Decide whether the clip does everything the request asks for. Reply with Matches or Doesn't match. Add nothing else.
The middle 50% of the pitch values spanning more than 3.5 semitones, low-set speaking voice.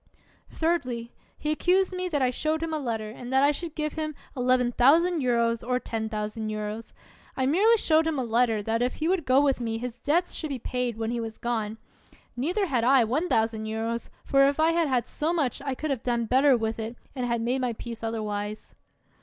Doesn't match